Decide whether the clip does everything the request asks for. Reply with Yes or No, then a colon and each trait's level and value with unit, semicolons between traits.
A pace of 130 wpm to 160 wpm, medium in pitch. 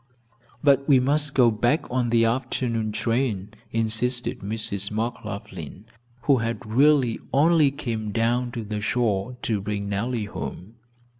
No: slow, 135 wpm; low, 115 Hz